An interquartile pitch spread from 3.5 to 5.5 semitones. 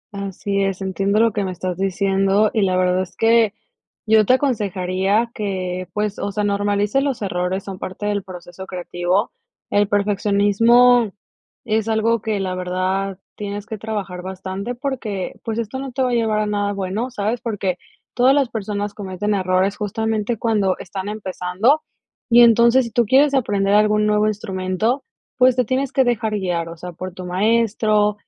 No: average, 2.9 semitones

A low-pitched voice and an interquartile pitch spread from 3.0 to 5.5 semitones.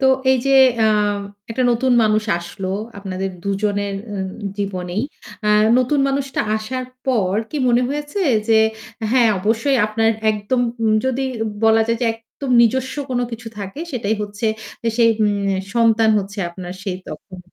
No: high, 225 Hz; average, 4.0 semitones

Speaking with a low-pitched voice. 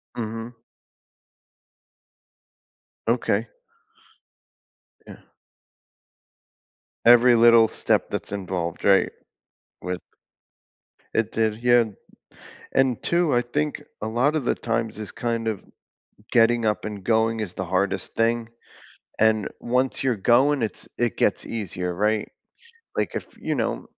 Yes: low, 115 Hz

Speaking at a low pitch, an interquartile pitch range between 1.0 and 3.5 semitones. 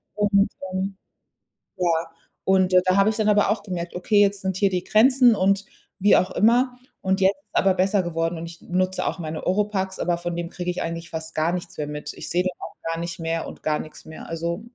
No: medium, 185 Hz; average, 2.9 semitones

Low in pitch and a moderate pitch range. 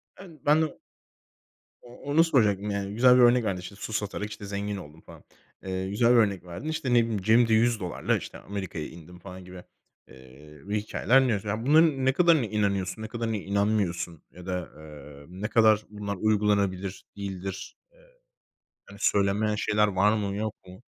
Yes: low, 105 Hz; average, 3.4 semitones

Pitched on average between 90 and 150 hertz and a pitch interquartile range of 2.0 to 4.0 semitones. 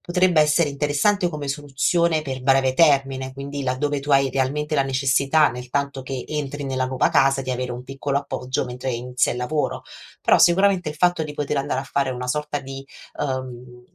Yes: low, 135 Hz; narrow, 2.3 semitones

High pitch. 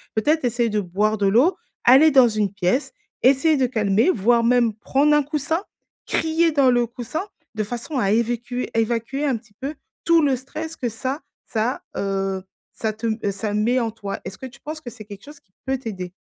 Yes: high, 240 Hz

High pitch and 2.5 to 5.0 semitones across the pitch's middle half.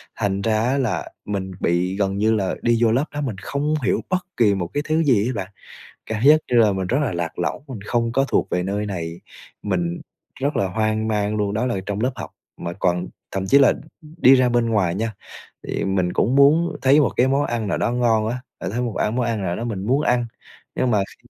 No: low, 110 Hz; average, 4.5 semitones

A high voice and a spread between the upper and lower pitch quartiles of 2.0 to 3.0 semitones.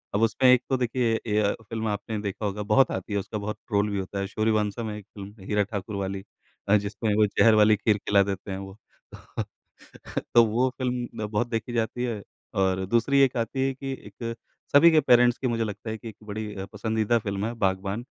No: low, 110 Hz; narrow, 2.6 semitones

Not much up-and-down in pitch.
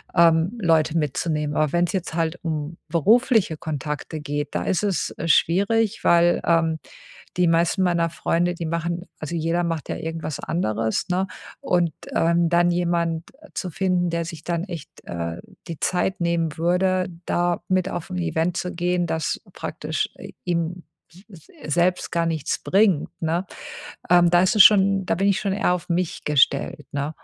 Yes: narrow, 1.9 semitones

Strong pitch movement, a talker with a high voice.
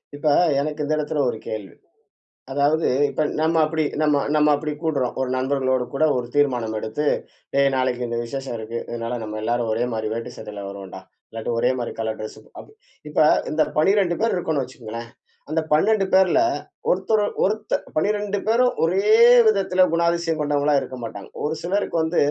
No: wide, 5.9 semitones; medium, 145 Hz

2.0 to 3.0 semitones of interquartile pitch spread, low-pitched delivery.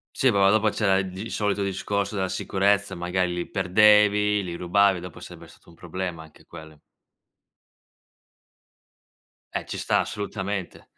Yes: narrow, 2.4 semitones; very low, 95 Hz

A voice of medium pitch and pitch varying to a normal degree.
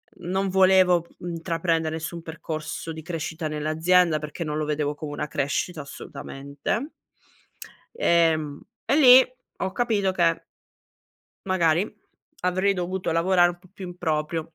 Yes: medium, 170 Hz; average, 3.0 semitones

